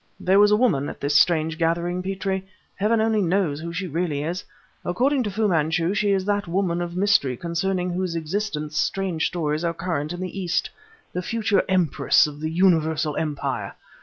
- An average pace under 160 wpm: No, average, 185 wpm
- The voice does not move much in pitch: No, average, 3.5 semitones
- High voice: No, medium, 175 Hz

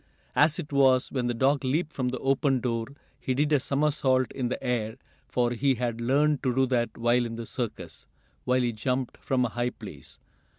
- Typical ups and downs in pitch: No, narrow, 2.2 semitones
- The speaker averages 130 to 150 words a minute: No, fast, 205 wpm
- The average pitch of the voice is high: No, low, 130 Hz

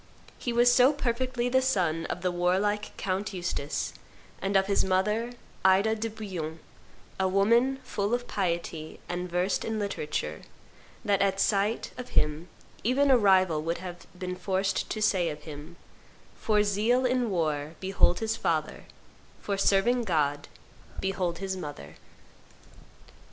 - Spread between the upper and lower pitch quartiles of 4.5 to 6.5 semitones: No, average, 3.9 semitones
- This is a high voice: Yes, high, 195 Hz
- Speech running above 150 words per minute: No, average, 145 wpm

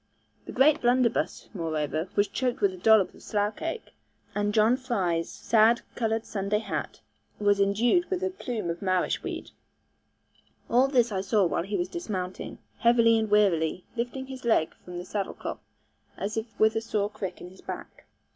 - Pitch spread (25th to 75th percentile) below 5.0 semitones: Yes, average, 3.8 semitones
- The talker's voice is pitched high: Yes, high, 215 Hz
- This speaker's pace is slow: No, average, 175 wpm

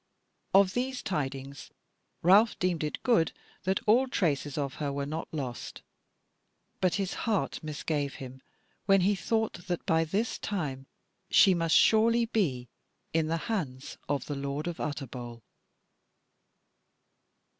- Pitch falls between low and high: Yes, medium, 165 Hz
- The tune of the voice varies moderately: No, wide, 6.0 semitones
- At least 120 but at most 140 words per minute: Yes, slow, 135 wpm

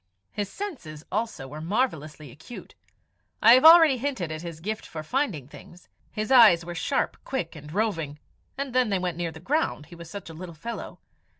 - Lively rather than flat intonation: Yes, wide, 7.5 semitones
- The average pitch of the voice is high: No, medium, 180 Hz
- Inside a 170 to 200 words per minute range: Yes, average, 190 wpm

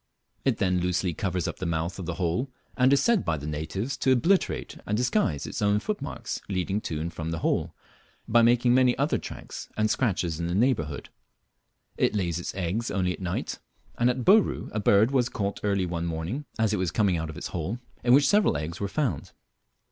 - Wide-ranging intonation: Yes, wide, 6.3 semitones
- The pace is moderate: No, fast, 210 wpm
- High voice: No, low, 100 Hz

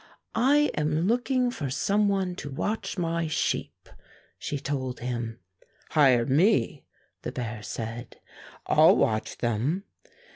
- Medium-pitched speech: Yes, medium, 145 Hz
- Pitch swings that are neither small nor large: No, wide, 8.6 semitones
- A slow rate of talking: Yes, slow, 120 wpm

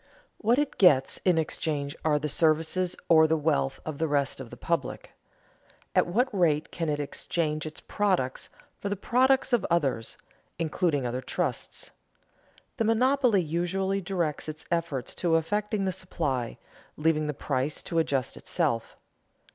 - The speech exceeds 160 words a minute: No, average, 150 wpm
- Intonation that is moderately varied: Yes, average, 4.3 semitones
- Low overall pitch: No, medium, 160 Hz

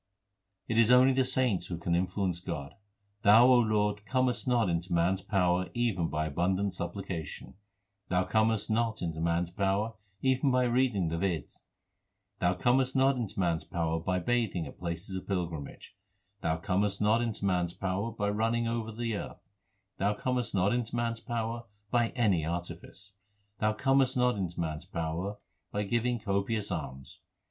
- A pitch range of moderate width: Yes, average, 5.0 semitones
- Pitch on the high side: No, low, 100 Hz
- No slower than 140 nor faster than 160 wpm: No, average, 170 wpm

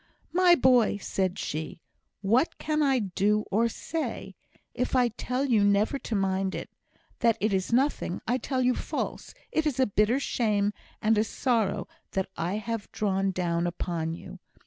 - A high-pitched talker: Yes, high, 215 Hz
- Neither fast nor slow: Yes, average, 170 wpm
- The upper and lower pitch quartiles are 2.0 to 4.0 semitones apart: No, average, 4.7 semitones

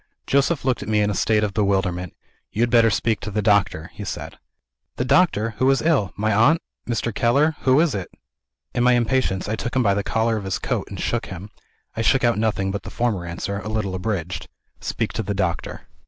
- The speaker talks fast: Yes, fast, 225 wpm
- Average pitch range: Yes, average, 3.6 semitones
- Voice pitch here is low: Yes, low, 110 Hz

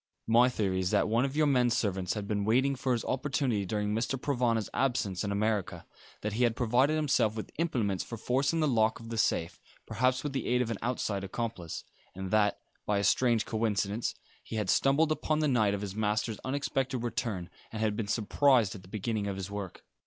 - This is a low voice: Yes, low, 115 Hz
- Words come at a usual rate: No, fast, 210 wpm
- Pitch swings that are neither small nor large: Yes, average, 3.9 semitones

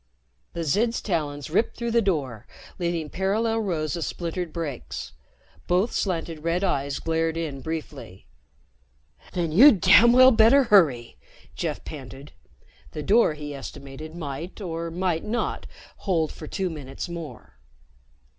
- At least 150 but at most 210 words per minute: No, slow, 135 wpm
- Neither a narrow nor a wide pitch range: Yes, average, 4.6 semitones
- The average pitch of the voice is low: No, medium, 165 Hz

